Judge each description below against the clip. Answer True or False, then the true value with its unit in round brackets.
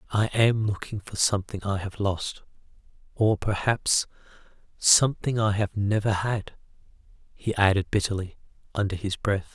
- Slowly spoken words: True (125 wpm)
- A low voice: True (105 Hz)